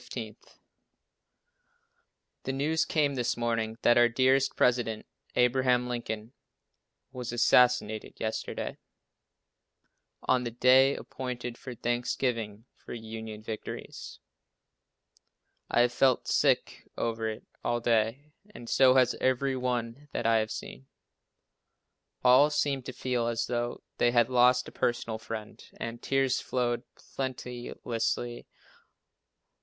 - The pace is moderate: No, slow, 115 wpm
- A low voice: Yes, low, 120 Hz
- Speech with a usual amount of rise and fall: No, narrow, 1.9 semitones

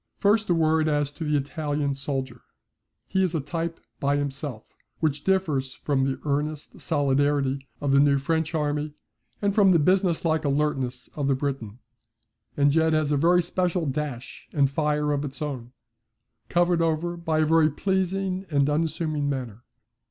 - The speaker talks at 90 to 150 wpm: No, average, 160 wpm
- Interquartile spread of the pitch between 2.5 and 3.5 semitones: Yes, average, 2.8 semitones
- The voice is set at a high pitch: No, medium, 150 Hz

